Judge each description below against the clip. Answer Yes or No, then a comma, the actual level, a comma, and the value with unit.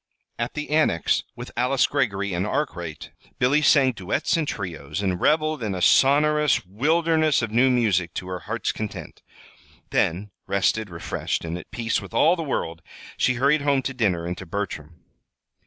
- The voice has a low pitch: Yes, low, 115 Hz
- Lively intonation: Yes, wide, 7.5 semitones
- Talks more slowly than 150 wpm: No, average, 170 wpm